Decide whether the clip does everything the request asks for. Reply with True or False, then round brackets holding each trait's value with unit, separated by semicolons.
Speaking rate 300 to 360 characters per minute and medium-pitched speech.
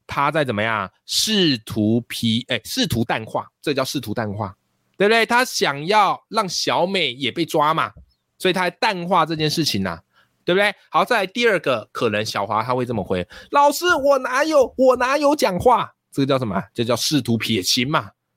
False (275 characters per minute; 150 Hz)